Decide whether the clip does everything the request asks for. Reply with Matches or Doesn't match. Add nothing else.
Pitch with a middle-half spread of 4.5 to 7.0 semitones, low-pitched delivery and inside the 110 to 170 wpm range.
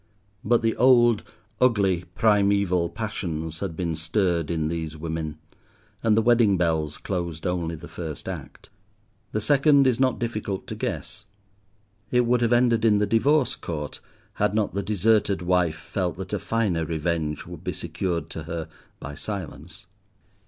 Matches